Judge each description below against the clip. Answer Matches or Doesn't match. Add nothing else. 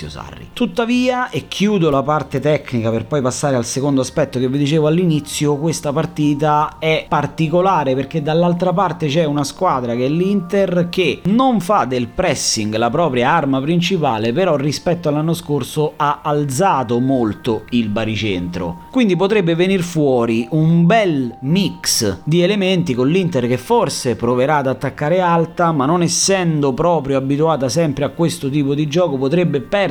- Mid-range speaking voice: Matches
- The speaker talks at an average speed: Matches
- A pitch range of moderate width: Matches